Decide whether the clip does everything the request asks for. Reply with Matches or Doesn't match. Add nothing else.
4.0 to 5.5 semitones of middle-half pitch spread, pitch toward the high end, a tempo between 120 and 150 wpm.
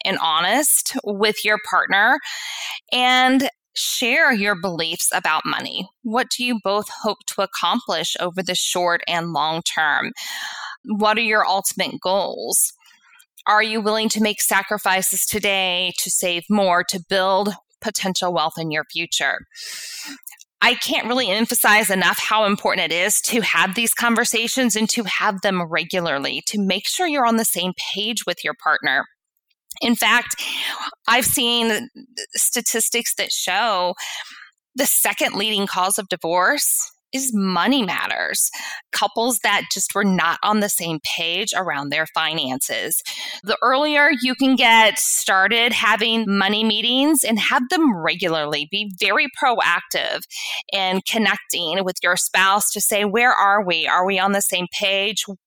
Matches